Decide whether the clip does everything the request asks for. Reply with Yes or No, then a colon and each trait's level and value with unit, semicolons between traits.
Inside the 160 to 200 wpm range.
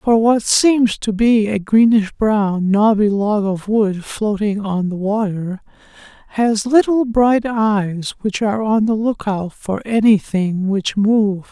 No: average, 150 wpm